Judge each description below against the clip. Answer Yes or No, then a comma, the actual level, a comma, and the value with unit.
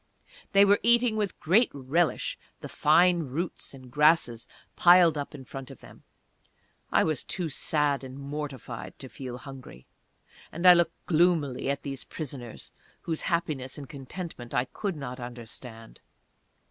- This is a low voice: No, medium, 145 Hz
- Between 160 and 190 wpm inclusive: No, average, 145 wpm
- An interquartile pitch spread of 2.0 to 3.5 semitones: No, average, 4.8 semitones